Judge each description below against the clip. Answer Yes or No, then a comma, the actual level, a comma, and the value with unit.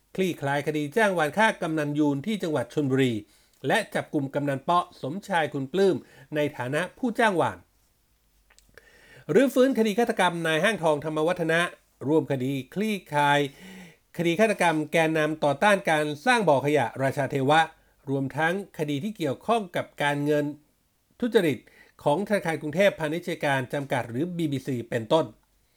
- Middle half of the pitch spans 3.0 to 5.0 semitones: Yes, average, 4.4 semitones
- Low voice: No, medium, 155 Hz